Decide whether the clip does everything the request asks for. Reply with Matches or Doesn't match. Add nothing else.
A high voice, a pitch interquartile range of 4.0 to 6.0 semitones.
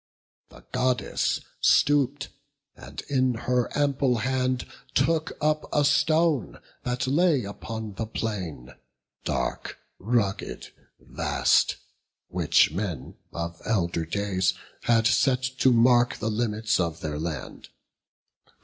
Doesn't match